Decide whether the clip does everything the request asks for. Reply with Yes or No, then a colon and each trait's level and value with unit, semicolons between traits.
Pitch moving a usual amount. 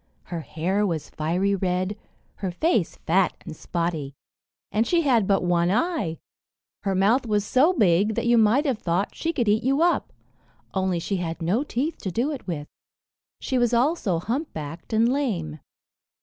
No: wide, 6.1 semitones